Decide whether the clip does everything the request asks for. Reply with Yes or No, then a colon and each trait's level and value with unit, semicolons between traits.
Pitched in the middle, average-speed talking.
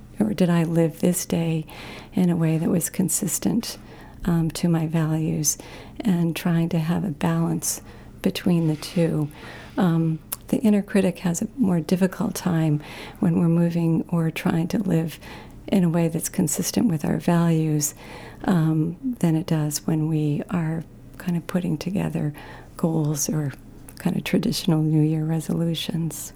Yes: medium, 165 Hz; average, 155 wpm